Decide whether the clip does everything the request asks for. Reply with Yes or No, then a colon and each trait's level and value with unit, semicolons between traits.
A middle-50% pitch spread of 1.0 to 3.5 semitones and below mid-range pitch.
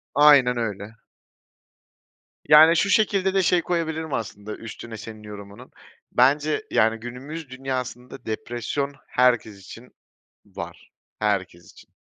No: wide, 5.5 semitones; low, 125 Hz